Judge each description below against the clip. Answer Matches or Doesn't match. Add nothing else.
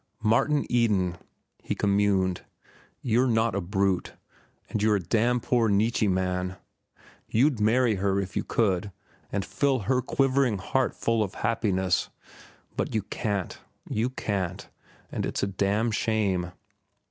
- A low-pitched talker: Matches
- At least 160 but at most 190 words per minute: Doesn't match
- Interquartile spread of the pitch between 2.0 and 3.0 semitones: Doesn't match